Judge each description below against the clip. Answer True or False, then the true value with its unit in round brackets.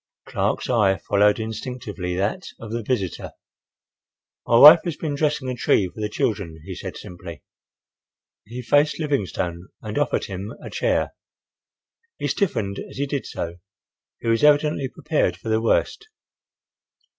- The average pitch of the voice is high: False (115 Hz)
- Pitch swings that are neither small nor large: False (6.3 semitones)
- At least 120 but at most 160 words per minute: True (145 wpm)